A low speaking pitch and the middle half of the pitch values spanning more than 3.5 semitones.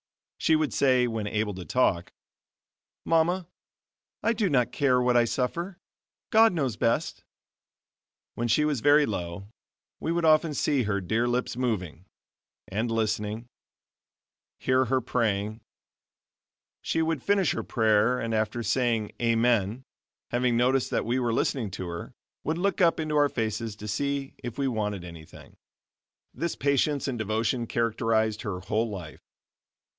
Yes: low, 120 Hz; average, 4.6 semitones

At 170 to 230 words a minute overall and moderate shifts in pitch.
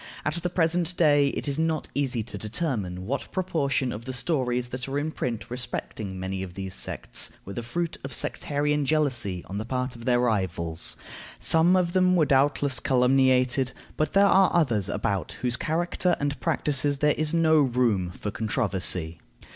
No: average, 175 wpm; wide, 5.7 semitones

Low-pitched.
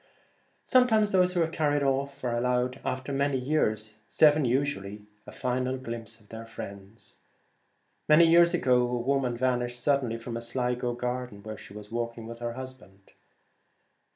Yes: low, 125 Hz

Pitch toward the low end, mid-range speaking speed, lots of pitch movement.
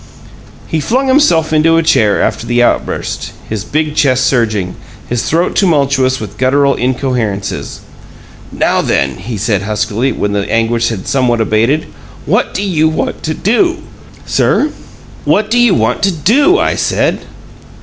Yes: low, 130 Hz; average, 150 wpm; wide, 6.6 semitones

